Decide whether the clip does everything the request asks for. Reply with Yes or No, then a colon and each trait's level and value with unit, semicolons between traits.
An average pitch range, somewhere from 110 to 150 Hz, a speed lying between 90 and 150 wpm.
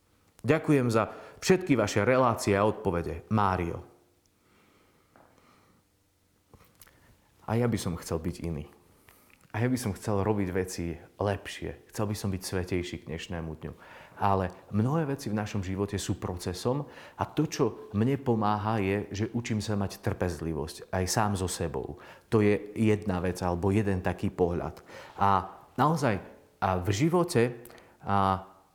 No: average, 3.1 semitones; low, 100 Hz; average, 140 wpm